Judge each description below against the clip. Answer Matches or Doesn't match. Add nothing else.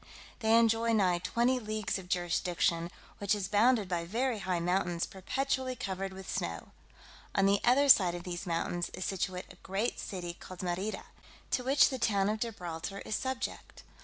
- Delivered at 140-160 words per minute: Doesn't match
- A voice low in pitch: Doesn't match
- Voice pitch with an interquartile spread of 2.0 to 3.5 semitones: Doesn't match